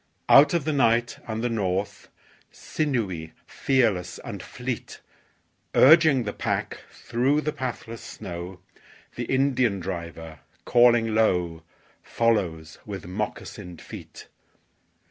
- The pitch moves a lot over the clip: Yes, wide, 6.2 semitones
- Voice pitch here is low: Yes, low, 115 Hz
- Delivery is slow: Yes, slow, 105 wpm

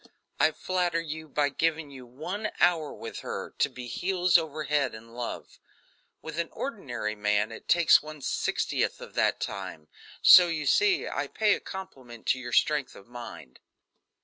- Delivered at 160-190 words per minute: Yes, average, 170 wpm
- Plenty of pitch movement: Yes, wide, 6.0 semitones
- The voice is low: No, medium, 150 Hz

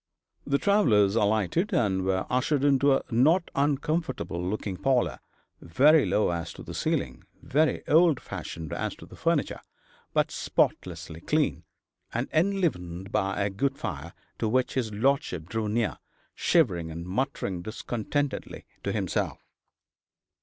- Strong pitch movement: Yes, wide, 6.9 semitones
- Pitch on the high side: No, low, 115 Hz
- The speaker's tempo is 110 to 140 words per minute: Yes, slow, 135 wpm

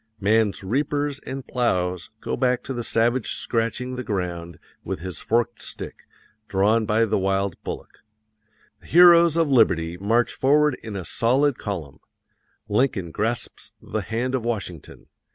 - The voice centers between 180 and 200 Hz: No, low, 115 Hz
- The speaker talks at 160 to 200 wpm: No, average, 145 wpm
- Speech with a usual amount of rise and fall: Yes, average, 4.9 semitones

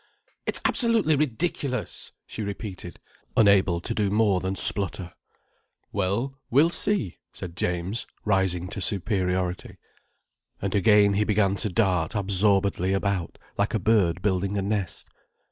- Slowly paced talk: Yes, slow, 130 wpm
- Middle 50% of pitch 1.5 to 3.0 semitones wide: Yes, narrow, 2.6 semitones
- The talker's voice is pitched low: Yes, low, 100 Hz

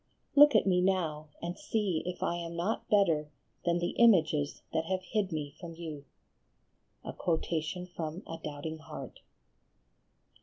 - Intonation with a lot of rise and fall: No, average, 2.9 semitones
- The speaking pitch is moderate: Yes, medium, 170 Hz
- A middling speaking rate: No, slow, 130 wpm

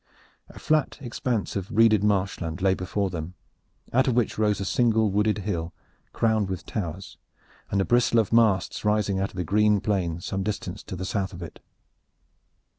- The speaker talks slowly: No, average, 180 wpm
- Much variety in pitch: No, average, 2.7 semitones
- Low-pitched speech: Yes, low, 100 Hz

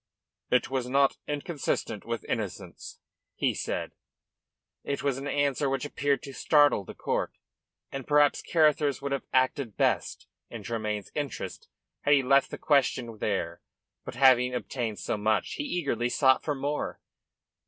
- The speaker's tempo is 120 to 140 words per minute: No, average, 150 wpm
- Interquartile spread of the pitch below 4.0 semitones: Yes, average, 2.9 semitones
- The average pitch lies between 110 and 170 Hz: Yes, low, 135 Hz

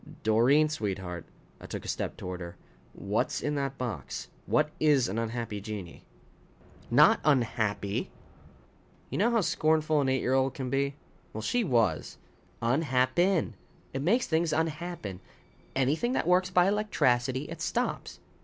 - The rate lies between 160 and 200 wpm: No, average, 150 wpm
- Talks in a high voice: No, low, 135 Hz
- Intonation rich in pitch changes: Yes, wide, 6.1 semitones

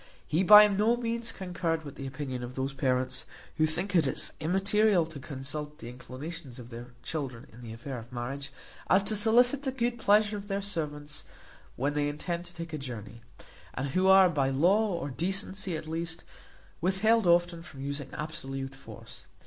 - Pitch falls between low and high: Yes, medium, 160 Hz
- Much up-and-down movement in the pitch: Yes, wide, 6.1 semitones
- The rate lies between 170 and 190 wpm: Yes, average, 180 wpm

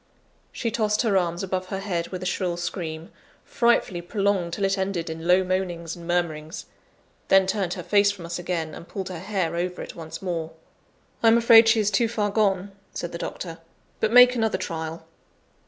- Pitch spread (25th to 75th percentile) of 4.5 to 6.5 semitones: No, average, 3.1 semitones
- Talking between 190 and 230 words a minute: Yes, average, 195 wpm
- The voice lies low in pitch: No, medium, 185 Hz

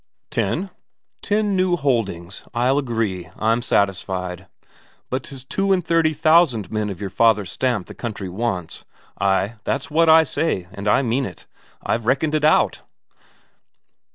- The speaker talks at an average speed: Yes, average, 150 wpm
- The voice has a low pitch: Yes, low, 120 Hz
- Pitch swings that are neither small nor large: No, wide, 7.8 semitones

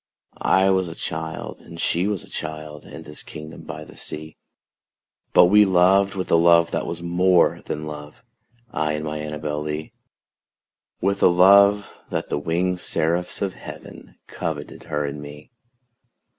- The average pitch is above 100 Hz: No, very low, 85 Hz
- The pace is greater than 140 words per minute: Yes, average, 160 wpm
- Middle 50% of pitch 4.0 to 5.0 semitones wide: No, average, 3.2 semitones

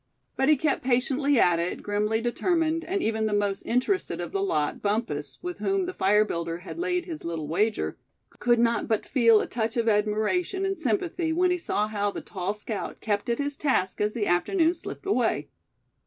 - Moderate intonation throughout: No, wide, 7.8 semitones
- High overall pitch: Yes, high, 230 Hz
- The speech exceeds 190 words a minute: Yes, average, 200 wpm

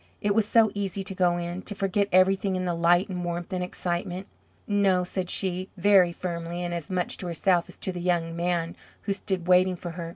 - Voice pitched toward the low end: No, medium, 180 Hz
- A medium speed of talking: No, fast, 220 wpm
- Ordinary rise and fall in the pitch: No, narrow, 1.8 semitones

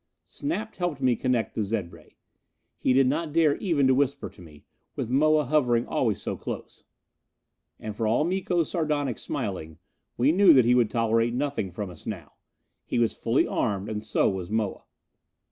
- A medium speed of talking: Yes, average, 180 wpm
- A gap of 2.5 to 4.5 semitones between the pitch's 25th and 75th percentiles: No, wide, 5.6 semitones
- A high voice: No, low, 125 Hz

